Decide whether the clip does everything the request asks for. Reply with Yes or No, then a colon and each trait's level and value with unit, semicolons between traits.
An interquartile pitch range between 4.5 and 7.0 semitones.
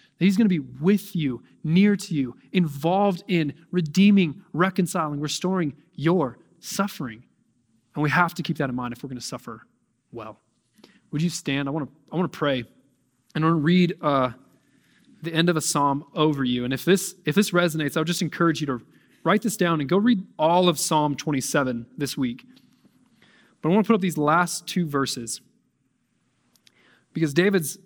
Yes: average, 4.8 semitones